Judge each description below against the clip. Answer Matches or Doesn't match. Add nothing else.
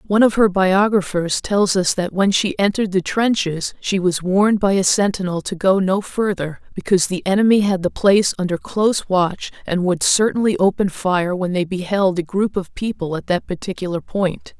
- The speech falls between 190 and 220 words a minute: Matches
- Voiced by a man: Doesn't match